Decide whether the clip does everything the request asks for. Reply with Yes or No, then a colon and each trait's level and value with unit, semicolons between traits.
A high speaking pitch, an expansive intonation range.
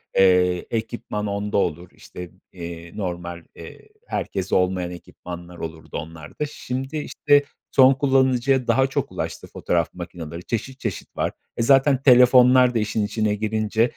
No: low, 105 Hz; wide, 6.3 semitones